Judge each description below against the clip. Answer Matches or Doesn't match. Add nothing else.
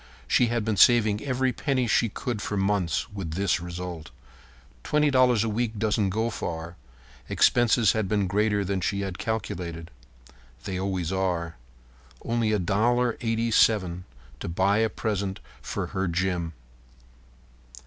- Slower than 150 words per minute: Matches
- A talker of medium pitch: Doesn't match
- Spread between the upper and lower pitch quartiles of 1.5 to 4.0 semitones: Matches